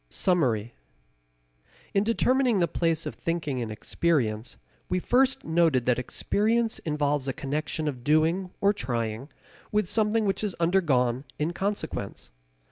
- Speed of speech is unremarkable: No, slow, 130 wpm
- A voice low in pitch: No, medium, 160 Hz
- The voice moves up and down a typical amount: No, wide, 7.4 semitones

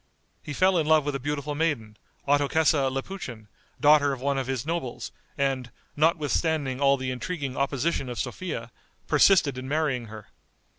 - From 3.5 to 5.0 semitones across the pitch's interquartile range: No, average, 3.1 semitones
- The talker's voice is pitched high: No, medium, 140 Hz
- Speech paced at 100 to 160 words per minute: Yes, average, 155 wpm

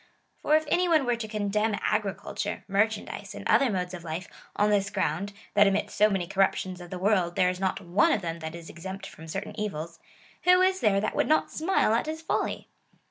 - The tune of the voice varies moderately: Yes, average, 3.6 semitones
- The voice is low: No, high, 200 Hz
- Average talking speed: No, fast, 220 wpm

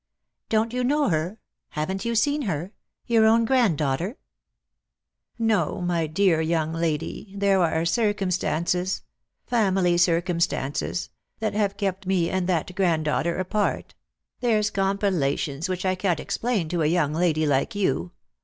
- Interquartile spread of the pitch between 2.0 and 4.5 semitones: Yes, average, 4.0 semitones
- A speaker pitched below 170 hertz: No, medium, 185 Hz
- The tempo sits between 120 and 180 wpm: Yes, average, 150 wpm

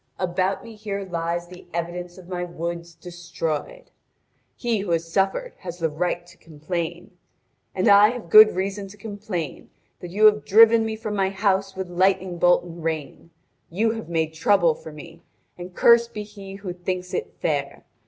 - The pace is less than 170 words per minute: No, average, 175 wpm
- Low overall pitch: No, medium, 180 Hz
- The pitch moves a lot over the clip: No, average, 3.1 semitones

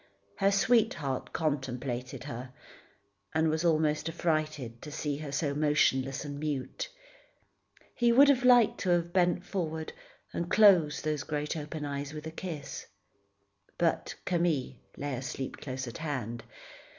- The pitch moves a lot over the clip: No, average, 3.5 semitones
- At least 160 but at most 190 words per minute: No, average, 140 wpm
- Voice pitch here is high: No, medium, 150 Hz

